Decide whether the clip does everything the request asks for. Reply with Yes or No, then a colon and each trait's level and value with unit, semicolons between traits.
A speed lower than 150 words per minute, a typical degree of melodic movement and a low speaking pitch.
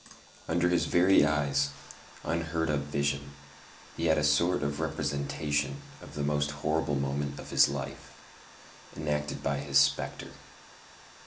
No: slow, 135 wpm; narrow, 1.6 semitones; very low, 75 Hz